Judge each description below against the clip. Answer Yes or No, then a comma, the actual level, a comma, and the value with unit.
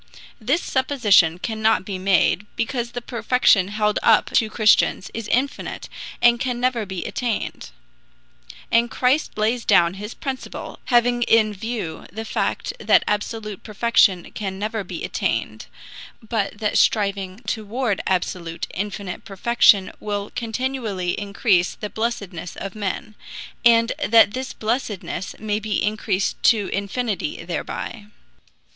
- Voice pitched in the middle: No, high, 215 Hz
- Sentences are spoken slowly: Yes, slow, 125 wpm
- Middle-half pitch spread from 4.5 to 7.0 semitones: No, average, 3.1 semitones